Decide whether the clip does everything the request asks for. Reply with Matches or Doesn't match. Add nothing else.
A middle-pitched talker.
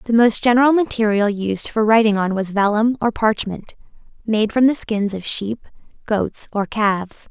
Doesn't match